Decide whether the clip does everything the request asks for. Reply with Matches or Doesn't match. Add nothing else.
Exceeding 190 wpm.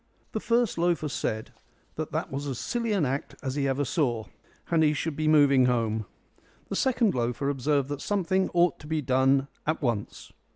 Doesn't match